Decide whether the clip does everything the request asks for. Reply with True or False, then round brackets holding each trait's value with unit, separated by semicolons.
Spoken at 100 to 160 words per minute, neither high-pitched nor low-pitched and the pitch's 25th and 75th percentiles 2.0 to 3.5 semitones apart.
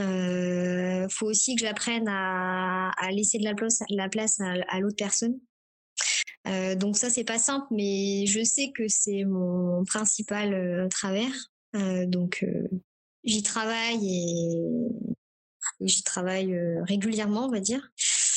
False (145 wpm; 200 Hz; 3.2 semitones)